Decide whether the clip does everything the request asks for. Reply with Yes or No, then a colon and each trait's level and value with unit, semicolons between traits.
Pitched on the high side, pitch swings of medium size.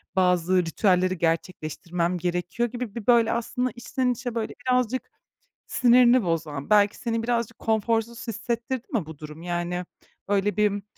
Yes: high, 210 Hz; average, 5.0 semitones